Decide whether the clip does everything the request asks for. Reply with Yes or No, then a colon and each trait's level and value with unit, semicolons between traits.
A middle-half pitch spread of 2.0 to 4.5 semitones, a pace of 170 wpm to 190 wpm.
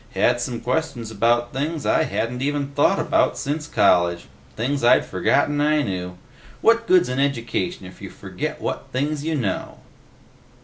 No: average, 4.2 semitones; average, 160 wpm